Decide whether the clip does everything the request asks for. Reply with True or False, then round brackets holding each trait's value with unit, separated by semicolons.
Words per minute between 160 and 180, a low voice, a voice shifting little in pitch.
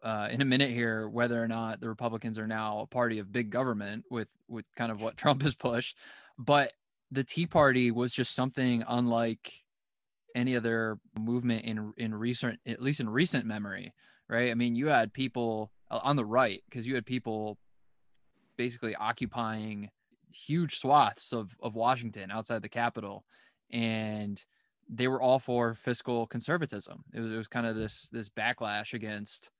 True (170 wpm; 115 Hz; 2.0 semitones)